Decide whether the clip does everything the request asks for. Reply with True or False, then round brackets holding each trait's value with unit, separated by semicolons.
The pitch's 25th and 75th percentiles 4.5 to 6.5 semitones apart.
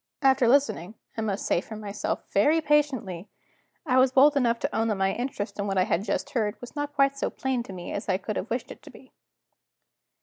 True (5.2 semitones)